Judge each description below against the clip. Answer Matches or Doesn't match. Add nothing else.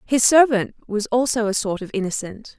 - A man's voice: Doesn't match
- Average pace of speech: Matches